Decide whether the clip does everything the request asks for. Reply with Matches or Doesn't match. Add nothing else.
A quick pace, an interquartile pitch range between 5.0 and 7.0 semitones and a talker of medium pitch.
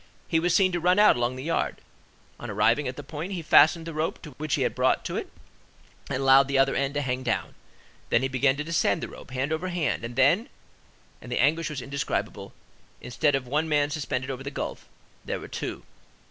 Doesn't match